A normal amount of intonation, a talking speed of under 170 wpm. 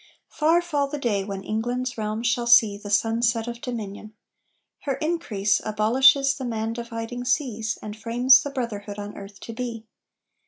Yes: average, 3.0 semitones; average, 160 wpm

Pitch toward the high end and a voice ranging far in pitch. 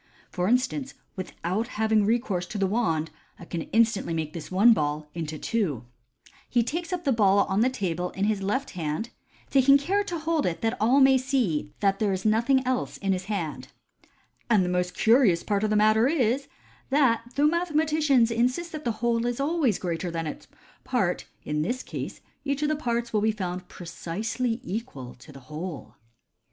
Yes: high, 220 Hz; wide, 6.3 semitones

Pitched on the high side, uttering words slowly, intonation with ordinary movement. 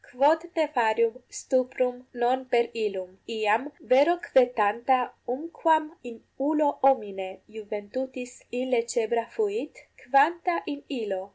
Yes: very high, 250 Hz; slow, 110 wpm; average, 4.4 semitones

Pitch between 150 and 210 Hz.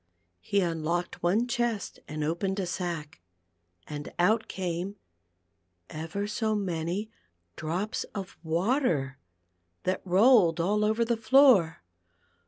Yes: medium, 185 Hz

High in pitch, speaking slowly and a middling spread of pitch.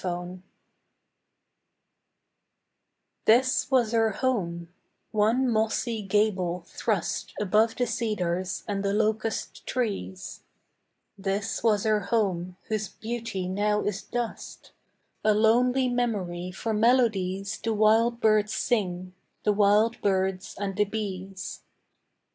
Yes: high, 210 Hz; slow, 105 wpm; average, 3.0 semitones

